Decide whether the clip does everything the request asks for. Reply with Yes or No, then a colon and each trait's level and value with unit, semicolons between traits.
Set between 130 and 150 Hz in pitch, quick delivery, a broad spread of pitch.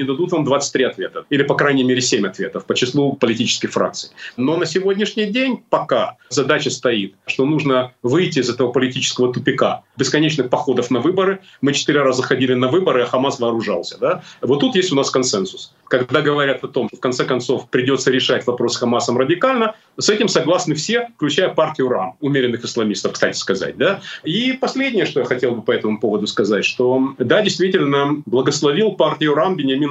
Yes: medium, 140 Hz; fast, 185 wpm; wide, 5.8 semitones